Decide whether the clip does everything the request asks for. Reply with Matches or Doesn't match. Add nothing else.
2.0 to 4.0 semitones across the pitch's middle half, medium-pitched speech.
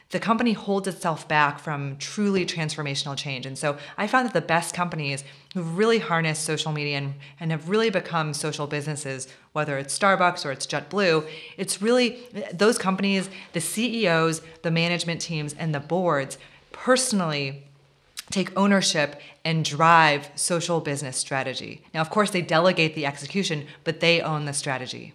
Doesn't match